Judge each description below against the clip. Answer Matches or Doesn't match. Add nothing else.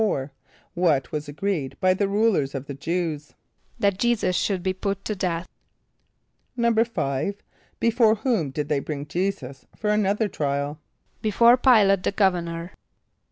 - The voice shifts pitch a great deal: Matches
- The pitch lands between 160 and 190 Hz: Matches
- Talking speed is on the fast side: Doesn't match